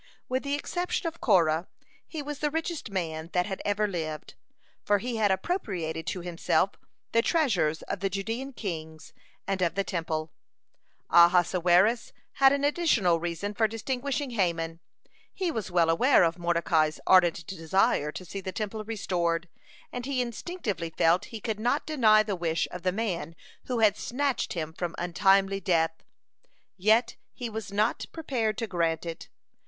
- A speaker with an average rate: Yes, average, 160 wpm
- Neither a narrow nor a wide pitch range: No, wide, 5.7 semitones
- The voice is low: No, high, 195 Hz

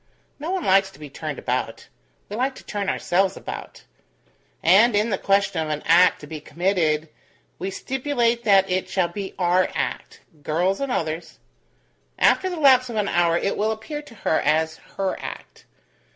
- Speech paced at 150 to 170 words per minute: No, average, 180 wpm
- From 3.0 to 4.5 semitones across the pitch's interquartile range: No, average, 5.2 semitones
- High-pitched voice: Yes, high, 195 Hz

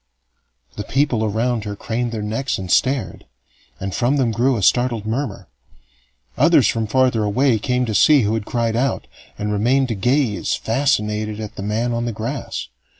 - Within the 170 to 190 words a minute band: Yes, average, 175 wpm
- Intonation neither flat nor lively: Yes, average, 3.1 semitones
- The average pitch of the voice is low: Yes, low, 115 Hz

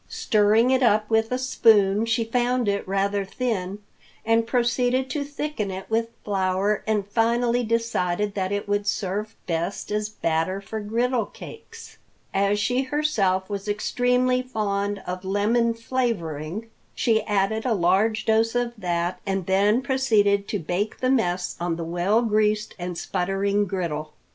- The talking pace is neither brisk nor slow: Yes, average, 150 wpm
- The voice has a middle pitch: No, high, 210 Hz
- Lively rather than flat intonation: No, average, 3.4 semitones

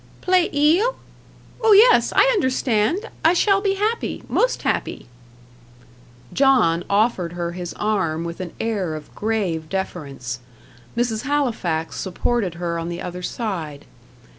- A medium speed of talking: No, slow, 130 wpm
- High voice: Yes, high, 210 Hz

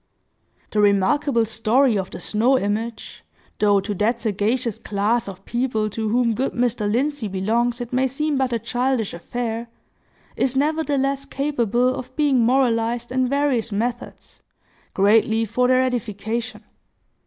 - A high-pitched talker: Yes, high, 235 Hz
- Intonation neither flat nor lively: Yes, average, 3.1 semitones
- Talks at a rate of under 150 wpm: Yes, average, 140 wpm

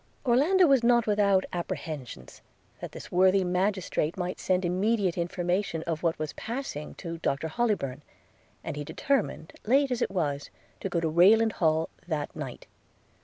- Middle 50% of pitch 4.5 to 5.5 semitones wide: Yes, average, 5.1 semitones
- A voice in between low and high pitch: Yes, medium, 180 Hz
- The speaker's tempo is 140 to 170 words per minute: Yes, average, 155 wpm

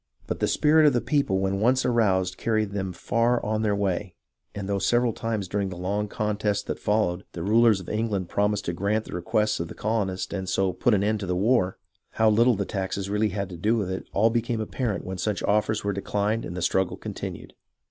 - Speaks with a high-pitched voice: No, low, 105 Hz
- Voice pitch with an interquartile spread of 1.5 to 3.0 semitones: Yes, narrow, 2.6 semitones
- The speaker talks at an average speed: No, fast, 230 wpm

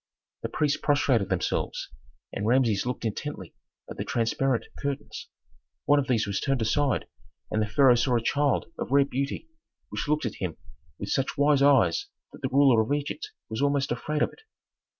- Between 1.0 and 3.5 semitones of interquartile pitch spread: No, average, 4.0 semitones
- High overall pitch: No, low, 135 Hz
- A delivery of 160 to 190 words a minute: Yes, average, 180 wpm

